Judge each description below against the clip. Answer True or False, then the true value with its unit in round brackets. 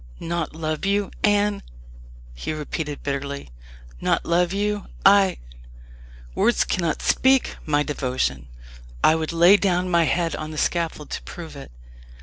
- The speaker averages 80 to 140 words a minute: True (135 wpm)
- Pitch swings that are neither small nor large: True (4.6 semitones)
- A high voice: False (170 Hz)